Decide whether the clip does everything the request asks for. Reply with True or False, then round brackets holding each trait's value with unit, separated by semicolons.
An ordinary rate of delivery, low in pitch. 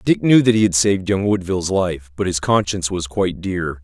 False (235 wpm; 95 Hz)